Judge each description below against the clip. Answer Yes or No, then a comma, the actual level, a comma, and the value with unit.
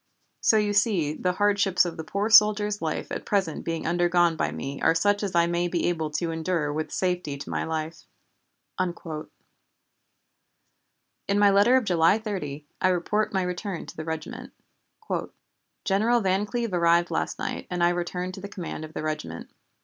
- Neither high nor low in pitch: Yes, medium, 175 Hz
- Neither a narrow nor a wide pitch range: Yes, average, 3.8 semitones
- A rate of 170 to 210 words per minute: Yes, average, 175 wpm